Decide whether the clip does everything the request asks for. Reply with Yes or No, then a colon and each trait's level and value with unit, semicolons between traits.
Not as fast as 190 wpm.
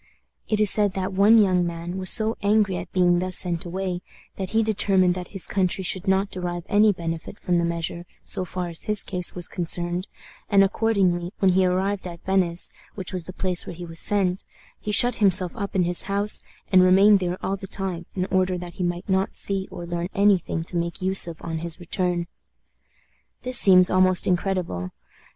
No: fast, 205 wpm